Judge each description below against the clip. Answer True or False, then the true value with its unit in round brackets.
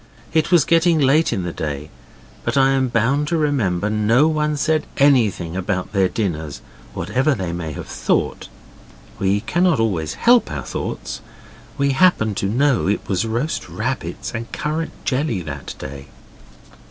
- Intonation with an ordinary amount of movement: False (8.1 semitones)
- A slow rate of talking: False (155 wpm)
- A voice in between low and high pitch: False (115 Hz)